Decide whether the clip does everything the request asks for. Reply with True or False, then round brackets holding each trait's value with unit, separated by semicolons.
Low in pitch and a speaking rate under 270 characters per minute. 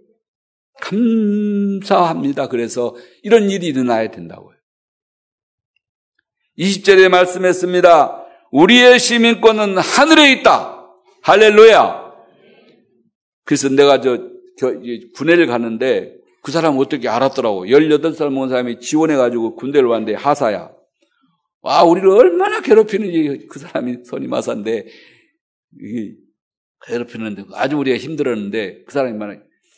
False (170 Hz; 260 characters per minute)